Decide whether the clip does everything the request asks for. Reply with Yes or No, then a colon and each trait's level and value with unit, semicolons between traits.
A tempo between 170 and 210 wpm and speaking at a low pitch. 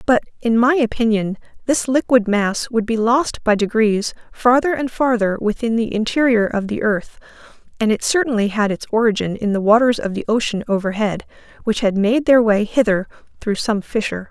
No: average, 180 wpm; high, 225 Hz